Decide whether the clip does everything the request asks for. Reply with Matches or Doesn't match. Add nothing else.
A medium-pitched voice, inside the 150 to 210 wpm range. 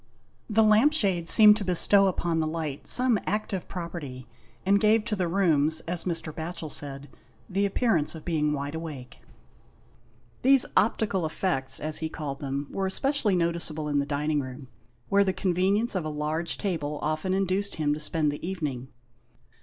Matches